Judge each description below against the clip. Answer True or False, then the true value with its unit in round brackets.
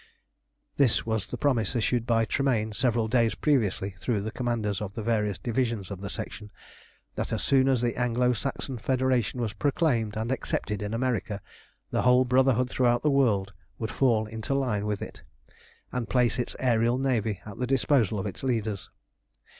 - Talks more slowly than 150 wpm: False (175 wpm)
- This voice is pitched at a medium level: False (115 Hz)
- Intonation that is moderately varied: True (3.1 semitones)